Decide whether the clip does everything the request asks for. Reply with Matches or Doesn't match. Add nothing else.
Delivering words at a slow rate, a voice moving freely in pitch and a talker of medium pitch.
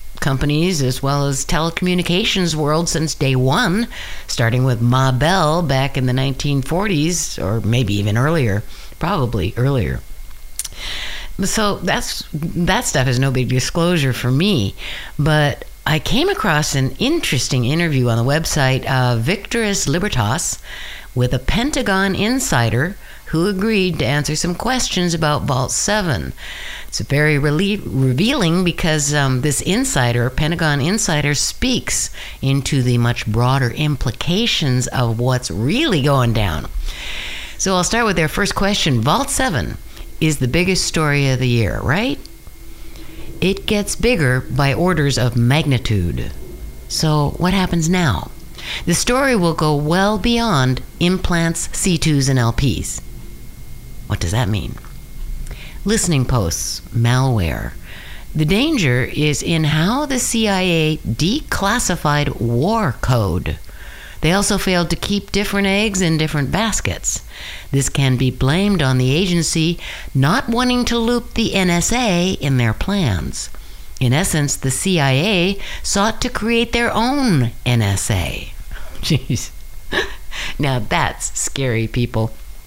Matches